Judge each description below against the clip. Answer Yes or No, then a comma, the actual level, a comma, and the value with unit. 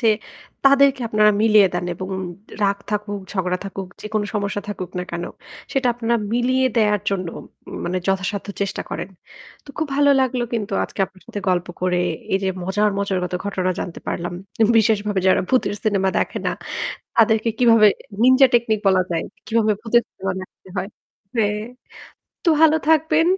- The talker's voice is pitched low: No, high, 210 Hz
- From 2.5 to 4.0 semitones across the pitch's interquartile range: Yes, average, 3.7 semitones